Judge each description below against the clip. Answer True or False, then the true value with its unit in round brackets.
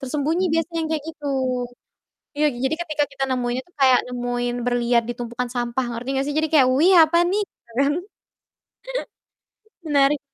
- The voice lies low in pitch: False (275 Hz)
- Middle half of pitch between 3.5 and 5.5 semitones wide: True (4.1 semitones)